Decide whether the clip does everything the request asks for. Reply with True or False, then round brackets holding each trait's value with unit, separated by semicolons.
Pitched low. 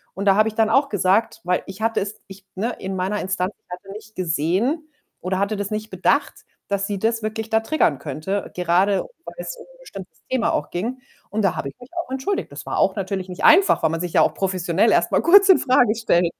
False (200 Hz)